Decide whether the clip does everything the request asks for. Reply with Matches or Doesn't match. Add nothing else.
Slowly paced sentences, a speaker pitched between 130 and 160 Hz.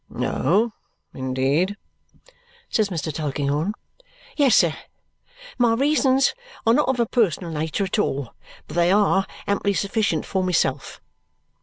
Doesn't match